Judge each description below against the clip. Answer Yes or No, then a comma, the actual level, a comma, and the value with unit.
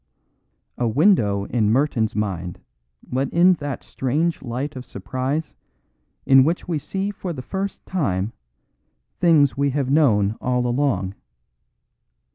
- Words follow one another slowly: Yes, slow, 125 wpm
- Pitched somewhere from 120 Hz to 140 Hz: Yes, low, 135 Hz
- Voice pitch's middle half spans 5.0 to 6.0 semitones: Yes, wide, 5.5 semitones